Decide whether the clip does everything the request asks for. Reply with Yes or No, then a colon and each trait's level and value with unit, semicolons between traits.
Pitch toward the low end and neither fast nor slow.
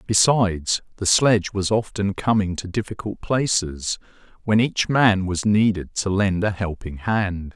Yes: low, 100 Hz; average, 150 wpm